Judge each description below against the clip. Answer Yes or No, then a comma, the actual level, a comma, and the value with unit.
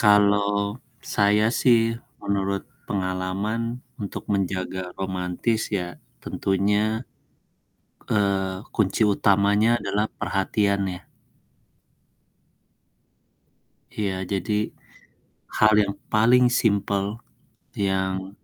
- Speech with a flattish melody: Yes, narrow, 1.7 semitones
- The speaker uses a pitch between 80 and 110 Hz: Yes, low, 100 Hz